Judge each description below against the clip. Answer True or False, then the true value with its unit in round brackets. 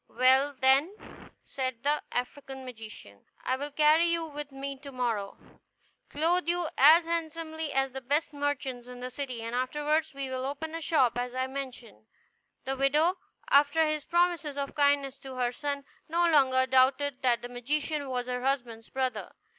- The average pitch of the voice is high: True (275 Hz)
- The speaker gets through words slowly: False (170 wpm)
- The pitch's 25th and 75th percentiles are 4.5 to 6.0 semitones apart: False (3.0 semitones)